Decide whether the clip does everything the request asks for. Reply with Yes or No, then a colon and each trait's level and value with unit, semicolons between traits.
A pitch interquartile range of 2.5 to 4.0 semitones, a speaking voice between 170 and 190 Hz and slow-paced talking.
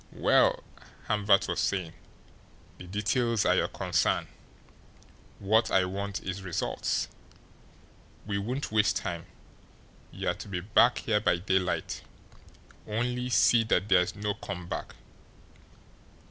No: average, 2.9 semitones; low, 100 Hz; slow, 120 wpm